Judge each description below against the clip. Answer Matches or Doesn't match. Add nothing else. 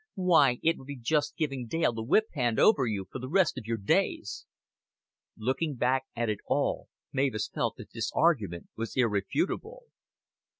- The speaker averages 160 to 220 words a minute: Matches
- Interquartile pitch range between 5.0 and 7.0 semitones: Matches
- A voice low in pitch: Matches